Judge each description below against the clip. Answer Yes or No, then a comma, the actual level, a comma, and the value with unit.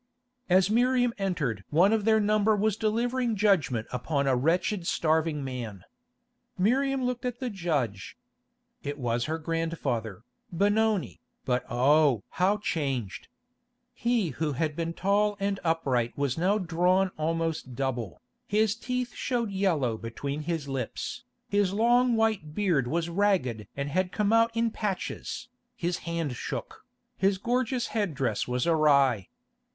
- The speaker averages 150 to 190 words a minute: No, average, 140 wpm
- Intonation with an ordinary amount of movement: No, wide, 7.2 semitones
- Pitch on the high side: No, medium, 170 Hz